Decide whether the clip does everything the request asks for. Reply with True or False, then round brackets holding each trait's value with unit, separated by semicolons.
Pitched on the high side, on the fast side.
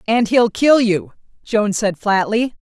False (215 Hz; 160 wpm)